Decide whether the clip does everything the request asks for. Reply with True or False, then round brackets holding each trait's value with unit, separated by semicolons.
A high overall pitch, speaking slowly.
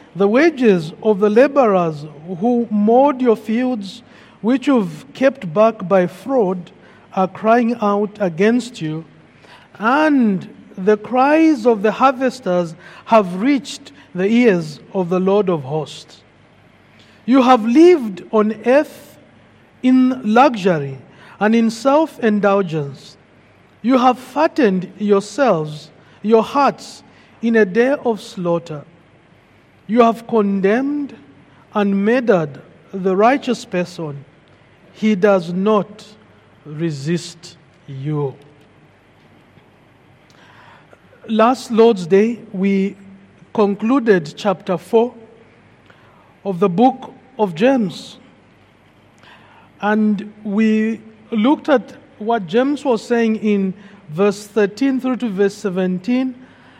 True (210 Hz; 100 wpm)